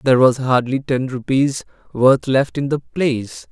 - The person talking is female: No, male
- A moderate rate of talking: Yes, average, 170 wpm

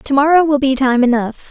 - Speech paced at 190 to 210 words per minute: Yes, average, 200 wpm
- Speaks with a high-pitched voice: Yes, very high, 270 Hz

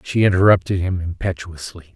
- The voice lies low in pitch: Yes, very low, 90 Hz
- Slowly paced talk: Yes, slow, 125 wpm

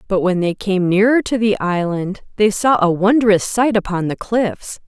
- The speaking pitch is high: Yes, high, 200 Hz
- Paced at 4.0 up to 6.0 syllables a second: Yes, 4.4 syllables/s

